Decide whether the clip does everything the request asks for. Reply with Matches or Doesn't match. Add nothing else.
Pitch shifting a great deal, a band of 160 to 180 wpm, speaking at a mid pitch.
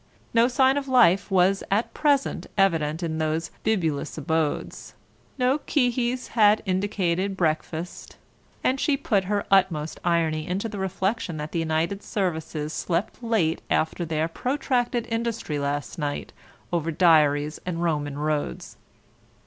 Doesn't match